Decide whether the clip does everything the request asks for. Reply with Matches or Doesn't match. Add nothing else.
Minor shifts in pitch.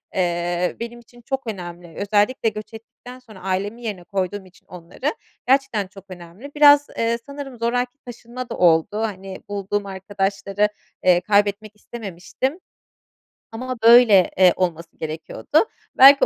Doesn't match